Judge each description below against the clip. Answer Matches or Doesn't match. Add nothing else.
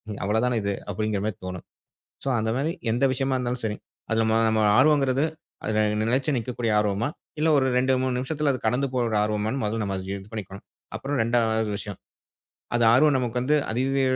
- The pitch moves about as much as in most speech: Matches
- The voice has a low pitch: Matches